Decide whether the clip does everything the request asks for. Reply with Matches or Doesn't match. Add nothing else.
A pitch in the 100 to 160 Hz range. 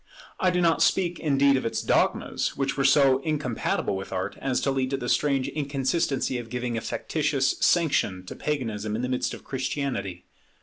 Matches